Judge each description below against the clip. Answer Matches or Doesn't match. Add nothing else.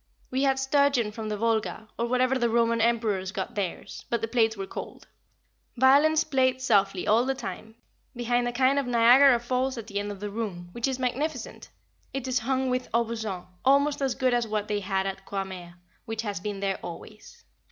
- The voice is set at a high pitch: Matches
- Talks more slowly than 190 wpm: Doesn't match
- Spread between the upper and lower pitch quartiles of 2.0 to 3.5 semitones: Doesn't match